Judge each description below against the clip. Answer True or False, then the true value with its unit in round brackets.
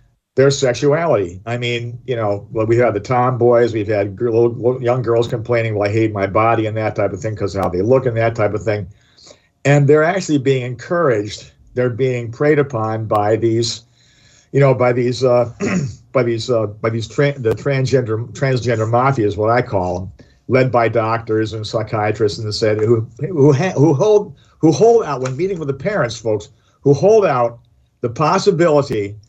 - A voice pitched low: True (120 Hz)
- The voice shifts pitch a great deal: False (3.5 semitones)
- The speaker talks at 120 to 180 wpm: False (200 wpm)